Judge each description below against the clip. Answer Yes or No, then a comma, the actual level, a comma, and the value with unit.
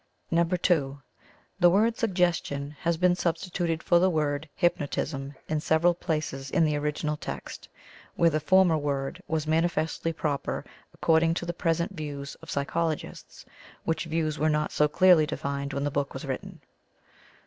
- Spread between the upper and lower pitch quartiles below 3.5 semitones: Yes, average, 2.8 semitones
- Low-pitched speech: No, medium, 160 Hz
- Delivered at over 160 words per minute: No, average, 150 wpm